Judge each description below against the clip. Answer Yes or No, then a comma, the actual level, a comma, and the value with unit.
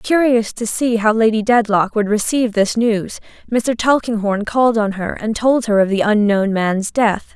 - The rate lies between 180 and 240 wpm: Yes, average, 190 wpm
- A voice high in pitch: Yes, high, 220 Hz